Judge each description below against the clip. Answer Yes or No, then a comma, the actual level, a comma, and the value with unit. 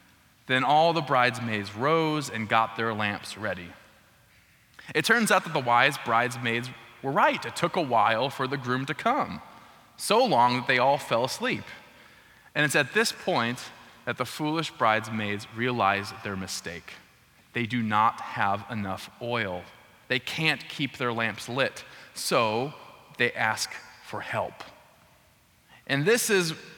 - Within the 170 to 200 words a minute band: No, average, 150 wpm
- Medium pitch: No, low, 120 Hz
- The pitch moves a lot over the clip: No, average, 4.0 semitones